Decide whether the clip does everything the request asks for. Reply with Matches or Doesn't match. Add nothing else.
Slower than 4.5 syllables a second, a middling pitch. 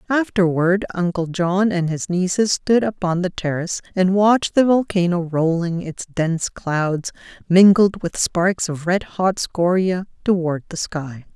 Matches